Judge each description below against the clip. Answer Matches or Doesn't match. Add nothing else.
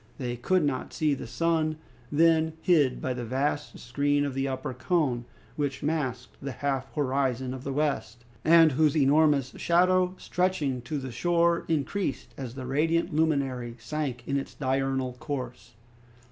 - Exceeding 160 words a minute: Doesn't match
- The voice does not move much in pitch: Doesn't match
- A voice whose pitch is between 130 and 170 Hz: Matches